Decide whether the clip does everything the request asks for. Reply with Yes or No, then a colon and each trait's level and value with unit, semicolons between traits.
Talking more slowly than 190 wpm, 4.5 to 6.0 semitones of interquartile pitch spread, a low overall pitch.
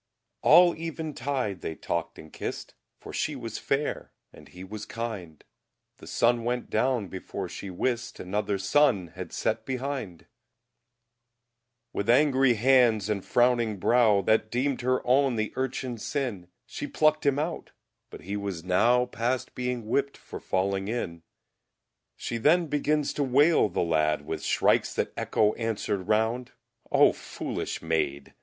Yes: average, 150 wpm; average, 5.2 semitones; low, 115 Hz